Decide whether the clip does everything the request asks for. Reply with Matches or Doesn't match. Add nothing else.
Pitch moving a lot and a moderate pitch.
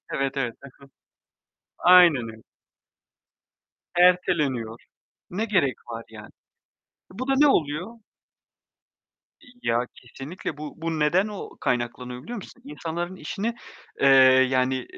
Matches